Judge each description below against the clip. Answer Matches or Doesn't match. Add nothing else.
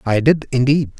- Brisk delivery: Doesn't match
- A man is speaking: Matches